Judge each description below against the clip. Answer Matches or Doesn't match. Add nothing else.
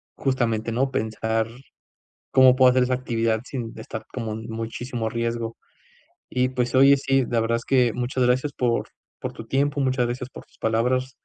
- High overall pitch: Doesn't match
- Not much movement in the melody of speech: Matches